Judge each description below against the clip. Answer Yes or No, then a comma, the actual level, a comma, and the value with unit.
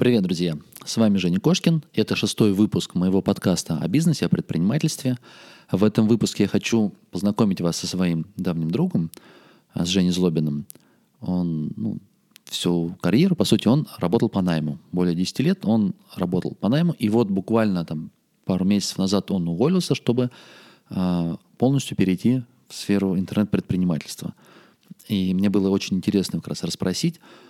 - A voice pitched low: Yes, low, 100 Hz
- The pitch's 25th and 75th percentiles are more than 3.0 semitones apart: Yes, average, 4.8 semitones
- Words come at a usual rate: Yes, average, 150 wpm